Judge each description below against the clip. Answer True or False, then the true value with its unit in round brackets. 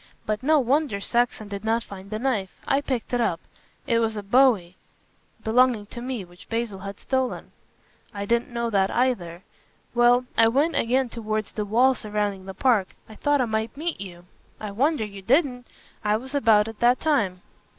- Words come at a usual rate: True (190 wpm)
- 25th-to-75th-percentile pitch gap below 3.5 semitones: False (3.8 semitones)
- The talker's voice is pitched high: True (230 Hz)